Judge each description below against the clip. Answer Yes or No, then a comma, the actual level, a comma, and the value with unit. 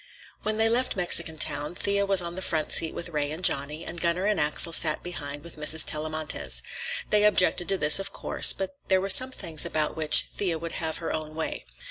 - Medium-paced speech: No, fast, 215 wpm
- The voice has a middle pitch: Yes, medium, 170 Hz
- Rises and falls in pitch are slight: No, average, 3.7 semitones